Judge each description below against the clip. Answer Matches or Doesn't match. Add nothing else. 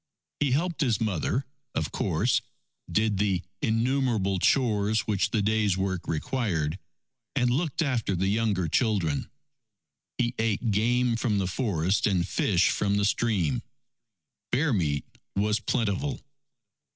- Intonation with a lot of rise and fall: Doesn't match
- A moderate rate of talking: Doesn't match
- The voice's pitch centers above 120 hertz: Doesn't match